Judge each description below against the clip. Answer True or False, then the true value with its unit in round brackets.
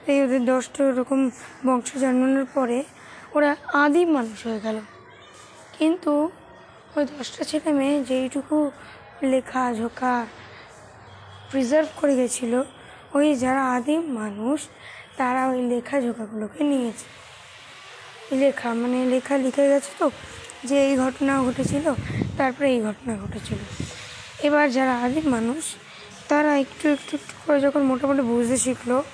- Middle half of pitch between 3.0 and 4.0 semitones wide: False (2.4 semitones)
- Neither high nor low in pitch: False (265 Hz)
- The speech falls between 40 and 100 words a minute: False (120 wpm)